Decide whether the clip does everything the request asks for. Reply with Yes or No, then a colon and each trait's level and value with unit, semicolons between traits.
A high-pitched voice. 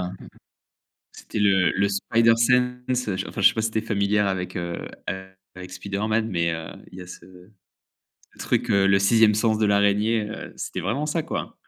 No: low, 100 Hz